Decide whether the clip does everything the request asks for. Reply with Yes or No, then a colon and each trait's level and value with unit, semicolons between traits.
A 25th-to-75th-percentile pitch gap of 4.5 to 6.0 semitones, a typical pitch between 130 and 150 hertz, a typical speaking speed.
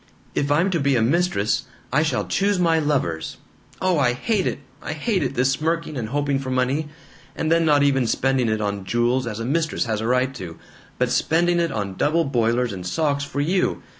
No: average, 5.2 semitones; medium, 140 Hz; fast, 210 wpm